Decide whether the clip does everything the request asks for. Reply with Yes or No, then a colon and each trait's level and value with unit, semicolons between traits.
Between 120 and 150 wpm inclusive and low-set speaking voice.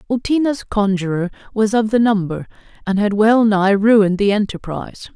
No: average, 140 wpm; high, 210 Hz